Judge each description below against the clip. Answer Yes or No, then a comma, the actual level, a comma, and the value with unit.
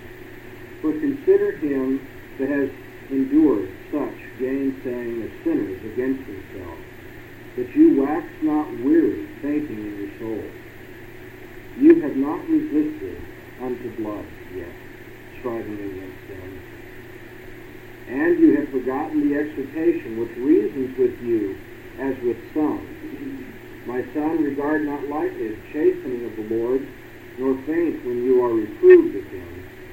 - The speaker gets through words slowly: Yes, slow, 125 wpm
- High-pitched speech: Yes, very high, 315 Hz